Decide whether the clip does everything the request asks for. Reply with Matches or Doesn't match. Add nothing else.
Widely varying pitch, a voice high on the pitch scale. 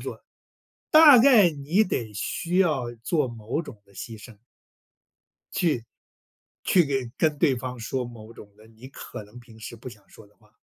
Doesn't match